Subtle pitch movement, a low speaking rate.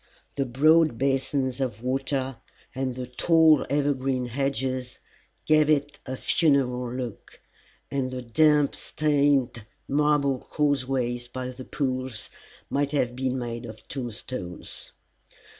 Yes: narrow, 2.3 semitones; slow, 115 wpm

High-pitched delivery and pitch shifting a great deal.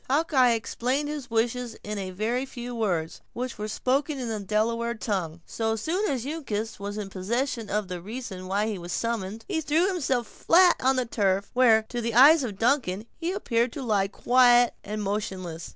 No: high, 230 Hz; average, 4.0 semitones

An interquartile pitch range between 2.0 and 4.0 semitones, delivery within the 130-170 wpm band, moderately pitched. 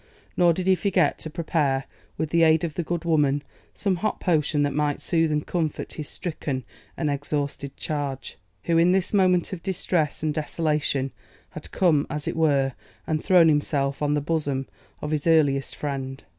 No: average, 2.8 semitones; average, 180 wpm; medium, 155 Hz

